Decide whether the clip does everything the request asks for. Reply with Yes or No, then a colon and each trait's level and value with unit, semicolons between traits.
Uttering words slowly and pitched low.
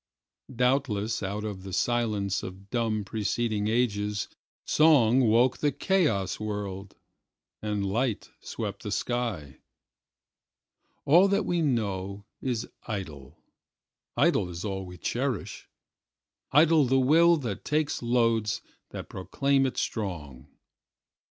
Yes: slow, 100 wpm; low, 110 Hz